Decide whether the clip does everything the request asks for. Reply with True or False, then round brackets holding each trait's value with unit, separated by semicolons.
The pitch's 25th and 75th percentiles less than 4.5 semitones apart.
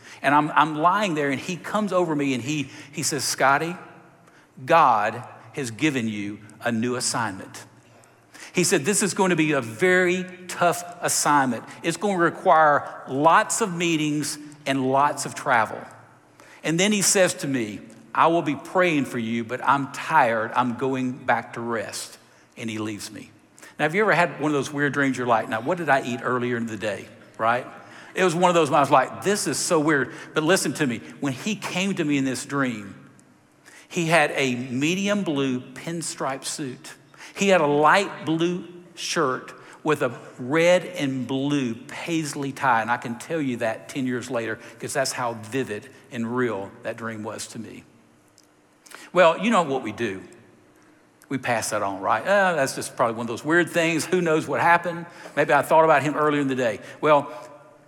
False (5.4 semitones)